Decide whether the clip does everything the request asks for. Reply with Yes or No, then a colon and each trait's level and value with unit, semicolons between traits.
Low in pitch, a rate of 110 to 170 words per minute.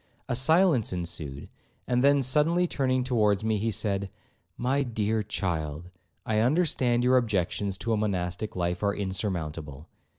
Yes: low, 110 Hz; average, 140 wpm